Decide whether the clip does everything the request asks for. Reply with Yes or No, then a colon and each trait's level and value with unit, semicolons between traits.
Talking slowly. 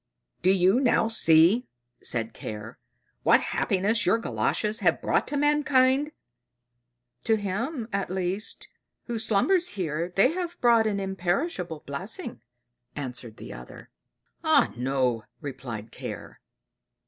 Yes: slow, 120 wpm